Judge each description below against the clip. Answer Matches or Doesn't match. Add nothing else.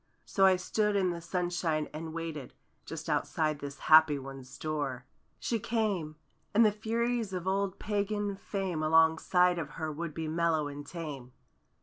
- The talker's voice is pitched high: Doesn't match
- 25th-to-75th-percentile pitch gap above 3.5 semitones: Matches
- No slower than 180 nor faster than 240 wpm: Doesn't match